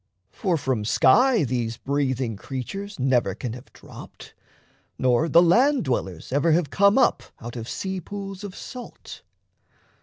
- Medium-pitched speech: Yes, medium, 145 Hz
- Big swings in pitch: Yes, wide, 8.1 semitones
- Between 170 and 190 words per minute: No, average, 145 wpm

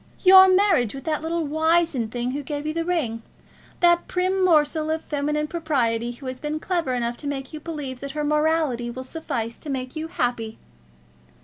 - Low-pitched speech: No, very high, 300 Hz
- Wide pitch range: No, average, 4.3 semitones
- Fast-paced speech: No, average, 190 wpm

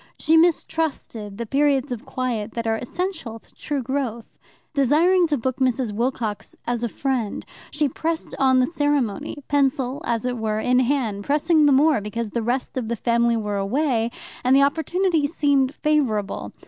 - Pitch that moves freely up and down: No, average, 4.1 semitones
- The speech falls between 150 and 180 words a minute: Yes, average, 170 wpm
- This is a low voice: No, very high, 260 Hz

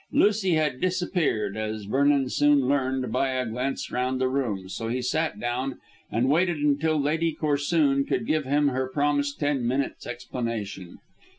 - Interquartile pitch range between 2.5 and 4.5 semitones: Yes, average, 2.9 semitones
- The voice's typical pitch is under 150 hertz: Yes, low, 135 Hz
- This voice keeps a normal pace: Yes, average, 160 wpm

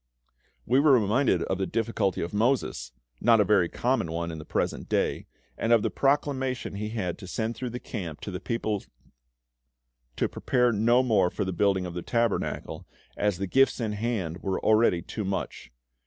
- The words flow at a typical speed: Yes, average, 185 wpm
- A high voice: No, low, 105 Hz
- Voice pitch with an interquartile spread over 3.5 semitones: Yes, average, 4.2 semitones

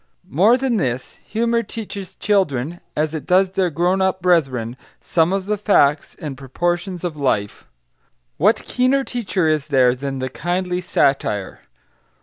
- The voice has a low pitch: No, medium, 175 Hz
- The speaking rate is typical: Yes, average, 145 wpm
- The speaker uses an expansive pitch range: Yes, wide, 5.7 semitones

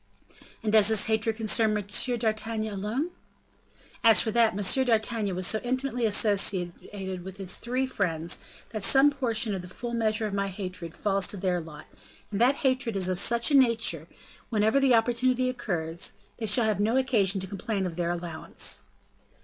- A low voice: No, high, 215 Hz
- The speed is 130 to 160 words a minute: No, average, 175 wpm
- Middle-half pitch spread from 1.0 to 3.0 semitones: No, average, 3.7 semitones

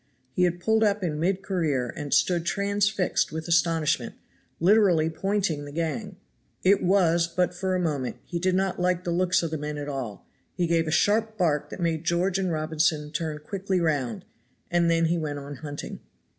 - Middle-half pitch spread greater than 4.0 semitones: No, average, 3.2 semitones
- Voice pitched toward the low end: No, medium, 170 Hz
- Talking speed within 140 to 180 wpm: No, average, 190 wpm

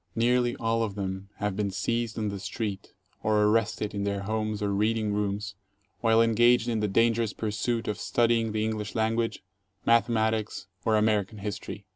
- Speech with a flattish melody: Yes, narrow, 1.7 semitones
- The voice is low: Yes, low, 110 Hz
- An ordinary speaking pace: Yes, average, 165 wpm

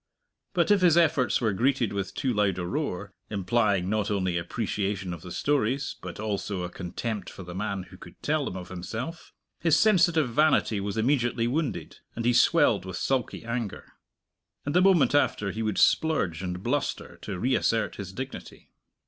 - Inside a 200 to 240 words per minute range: No, average, 175 wpm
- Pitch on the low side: Yes, low, 110 Hz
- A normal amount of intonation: No, wide, 6.5 semitones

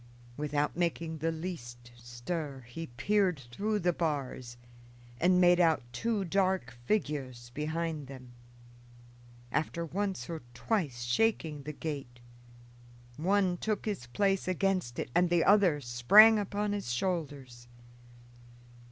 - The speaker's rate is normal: No, slow, 120 wpm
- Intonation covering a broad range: Yes, wide, 6.6 semitones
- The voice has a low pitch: No, medium, 165 Hz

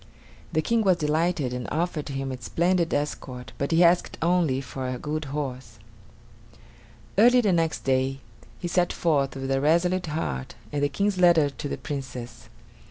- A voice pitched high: No, medium, 150 Hz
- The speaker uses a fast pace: No, average, 165 wpm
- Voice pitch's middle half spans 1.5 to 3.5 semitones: No, average, 4.3 semitones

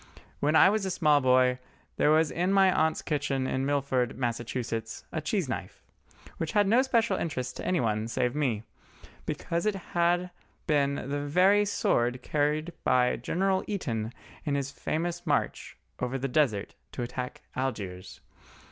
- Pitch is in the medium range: Yes, medium, 145 Hz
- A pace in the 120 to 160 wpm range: Yes, average, 155 wpm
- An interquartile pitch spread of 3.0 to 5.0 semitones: No, wide, 5.6 semitones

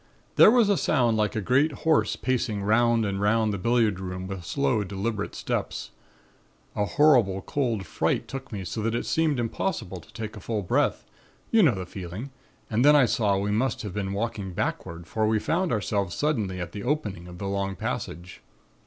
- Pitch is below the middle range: Yes, low, 110 Hz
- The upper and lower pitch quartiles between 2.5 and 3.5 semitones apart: No, average, 4.5 semitones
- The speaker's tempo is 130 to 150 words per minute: No, average, 195 wpm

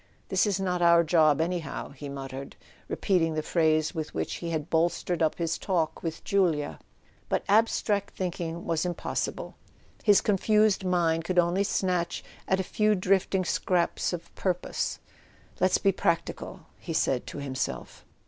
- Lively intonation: No, average, 2.9 semitones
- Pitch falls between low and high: Yes, medium, 175 Hz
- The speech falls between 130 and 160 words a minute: Yes, average, 155 wpm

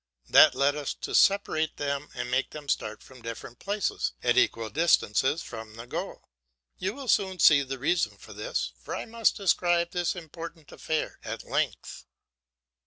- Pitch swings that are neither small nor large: No, wide, 5.8 semitones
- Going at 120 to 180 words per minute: Yes, average, 170 wpm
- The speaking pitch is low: No, medium, 150 Hz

